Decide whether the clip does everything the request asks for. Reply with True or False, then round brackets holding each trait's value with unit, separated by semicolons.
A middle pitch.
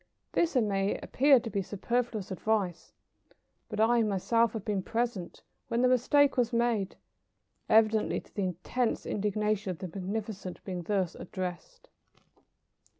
False (215 Hz)